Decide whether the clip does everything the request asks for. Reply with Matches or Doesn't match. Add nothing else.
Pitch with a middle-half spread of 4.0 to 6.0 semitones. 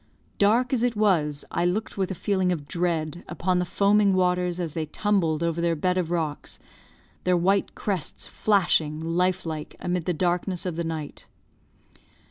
Doesn't match